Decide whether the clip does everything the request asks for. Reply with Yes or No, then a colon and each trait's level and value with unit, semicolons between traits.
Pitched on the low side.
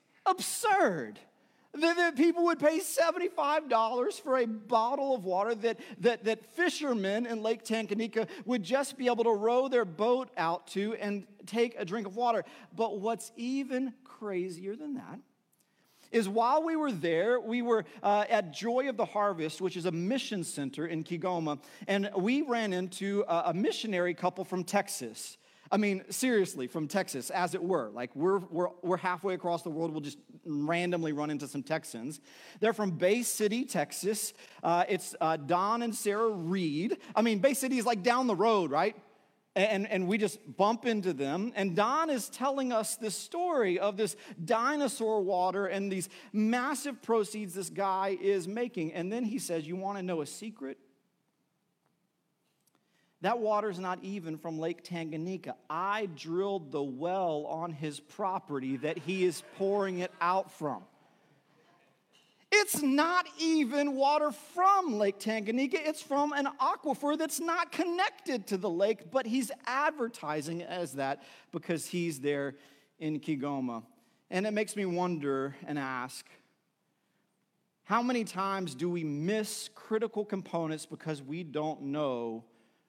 No: high, 200 Hz